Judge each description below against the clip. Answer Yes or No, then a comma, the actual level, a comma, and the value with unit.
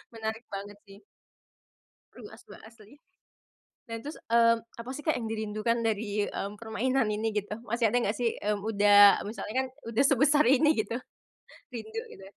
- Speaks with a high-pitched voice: Yes, high, 225 Hz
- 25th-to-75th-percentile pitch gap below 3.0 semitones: Yes, narrow, 2.5 semitones